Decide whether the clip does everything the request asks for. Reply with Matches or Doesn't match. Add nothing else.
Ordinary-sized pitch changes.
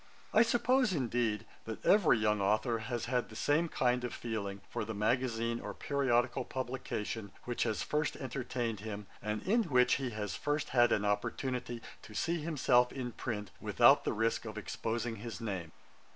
Matches